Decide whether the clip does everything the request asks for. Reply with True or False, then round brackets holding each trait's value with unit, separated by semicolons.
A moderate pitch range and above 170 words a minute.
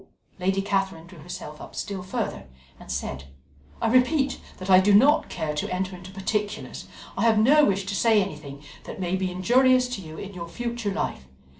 True (3.9 semitones; 190 wpm)